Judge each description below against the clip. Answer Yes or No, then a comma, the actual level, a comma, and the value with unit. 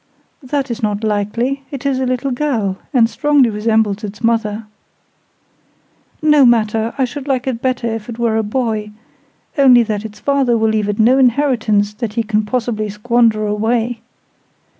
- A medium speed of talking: Yes, average, 160 wpm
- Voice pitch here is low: No, high, 230 Hz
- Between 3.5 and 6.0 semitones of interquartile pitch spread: No, average, 3.1 semitones